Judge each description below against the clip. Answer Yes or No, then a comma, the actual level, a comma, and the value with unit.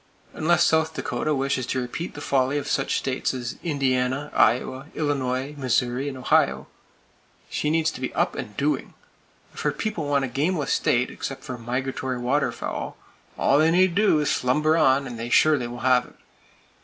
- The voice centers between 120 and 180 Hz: Yes, low, 135 Hz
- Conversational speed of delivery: Yes, average, 180 wpm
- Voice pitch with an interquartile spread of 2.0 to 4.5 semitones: Yes, average, 3.1 semitones